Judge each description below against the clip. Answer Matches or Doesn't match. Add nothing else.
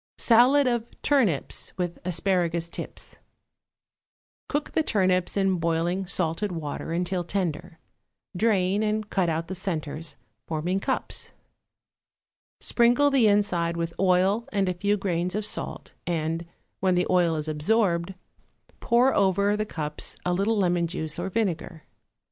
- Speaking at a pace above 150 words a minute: Doesn't match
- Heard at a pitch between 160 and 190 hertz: Matches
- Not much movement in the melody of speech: Doesn't match